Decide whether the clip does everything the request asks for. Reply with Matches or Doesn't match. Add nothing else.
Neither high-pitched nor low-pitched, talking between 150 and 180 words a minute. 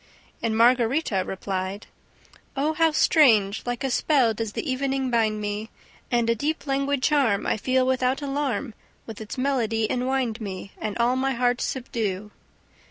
Doesn't match